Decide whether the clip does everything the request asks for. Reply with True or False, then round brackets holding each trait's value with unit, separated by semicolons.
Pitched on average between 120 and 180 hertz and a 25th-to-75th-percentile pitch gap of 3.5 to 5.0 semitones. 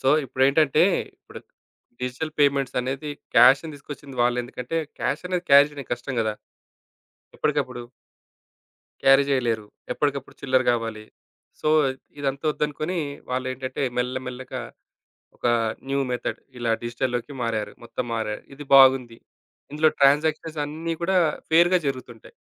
False (135 Hz; 3.1 semitones)